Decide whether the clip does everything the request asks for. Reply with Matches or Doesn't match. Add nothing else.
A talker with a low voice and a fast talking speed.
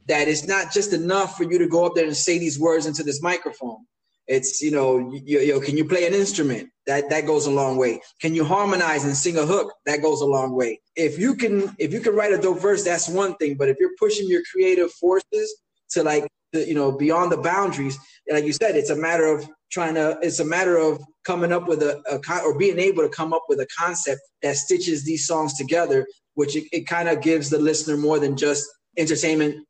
Doesn't match